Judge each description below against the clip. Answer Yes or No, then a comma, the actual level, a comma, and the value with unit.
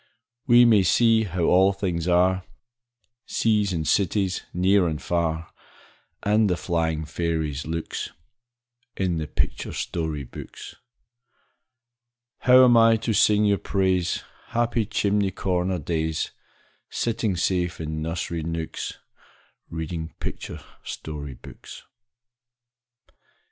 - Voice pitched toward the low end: Yes, very low, 90 Hz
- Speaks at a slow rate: Yes, slow, 110 wpm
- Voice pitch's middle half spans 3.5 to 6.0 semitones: Yes, average, 4.0 semitones